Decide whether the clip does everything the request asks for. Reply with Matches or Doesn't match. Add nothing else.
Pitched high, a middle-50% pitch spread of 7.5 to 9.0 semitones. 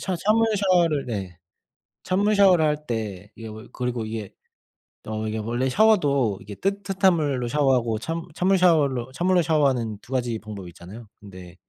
Doesn't match